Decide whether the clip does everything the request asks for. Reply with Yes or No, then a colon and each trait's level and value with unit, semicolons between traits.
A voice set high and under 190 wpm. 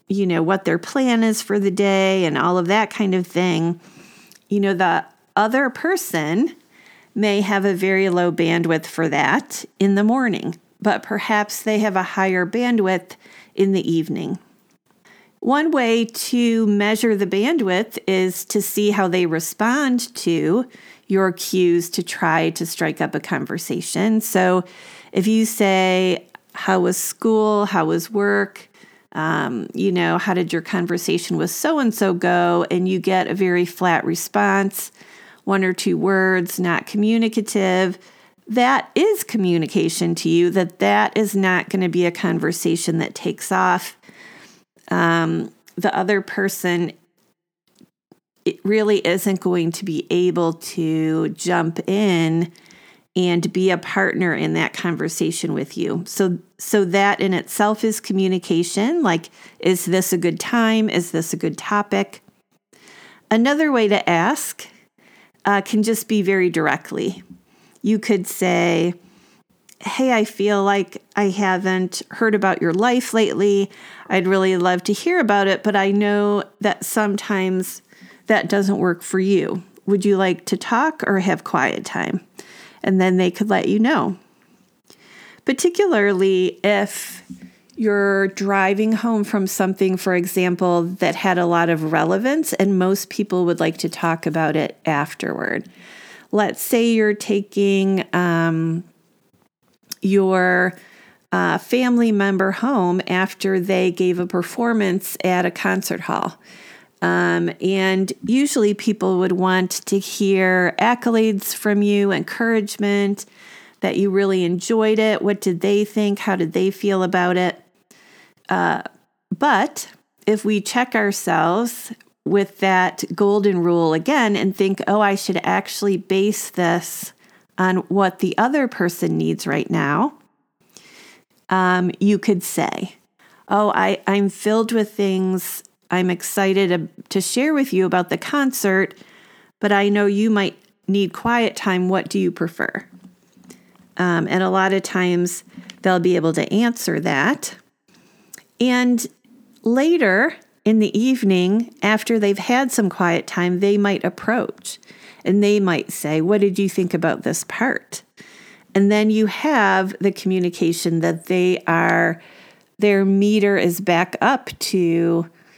Yes: high, 195 Hz; average, 145 wpm